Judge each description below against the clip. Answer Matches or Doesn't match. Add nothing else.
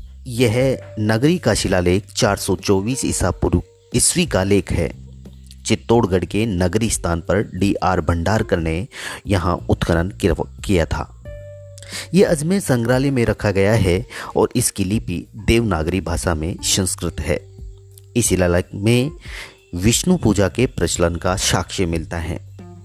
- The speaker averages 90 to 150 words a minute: Matches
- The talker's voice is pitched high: Doesn't match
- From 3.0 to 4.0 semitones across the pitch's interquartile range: Doesn't match